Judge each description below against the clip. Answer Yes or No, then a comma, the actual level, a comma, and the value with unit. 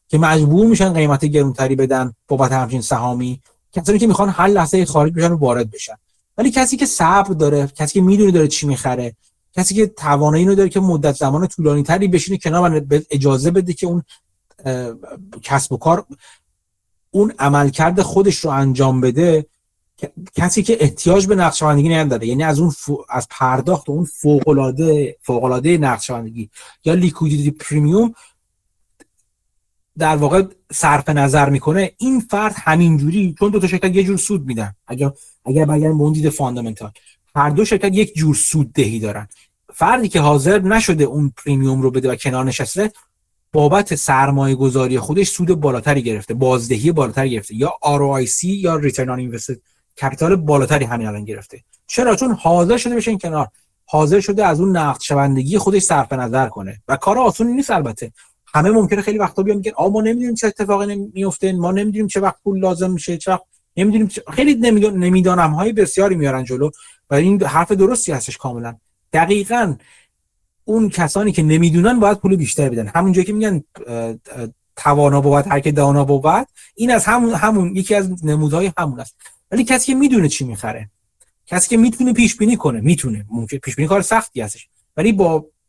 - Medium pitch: Yes, medium, 155 Hz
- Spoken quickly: Yes, fast, 170 wpm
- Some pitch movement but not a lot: No, wide, 6.4 semitones